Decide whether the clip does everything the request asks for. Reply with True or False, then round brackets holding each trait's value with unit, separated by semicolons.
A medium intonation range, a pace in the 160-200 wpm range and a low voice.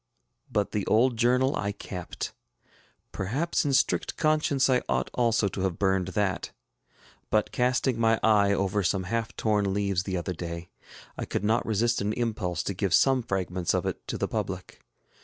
True (3.8 semitones; 175 wpm; 105 Hz)